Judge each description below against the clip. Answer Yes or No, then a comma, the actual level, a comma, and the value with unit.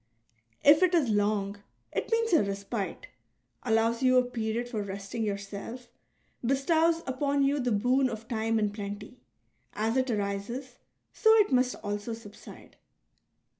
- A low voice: No, high, 230 Hz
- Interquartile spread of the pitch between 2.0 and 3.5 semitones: No, average, 4.2 semitones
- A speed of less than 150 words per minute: Yes, average, 140 wpm